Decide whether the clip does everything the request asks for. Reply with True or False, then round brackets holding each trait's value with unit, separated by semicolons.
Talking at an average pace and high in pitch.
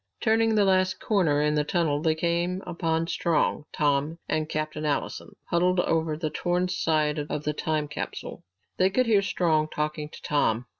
False (170 wpm; 160 Hz)